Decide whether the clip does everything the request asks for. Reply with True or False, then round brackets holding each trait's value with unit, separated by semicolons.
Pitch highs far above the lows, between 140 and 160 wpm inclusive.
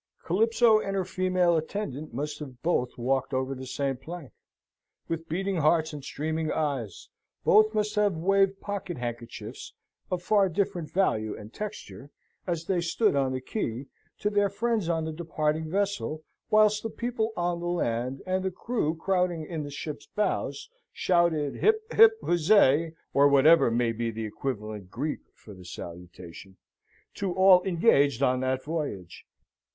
True (6.5 semitones; 155 wpm)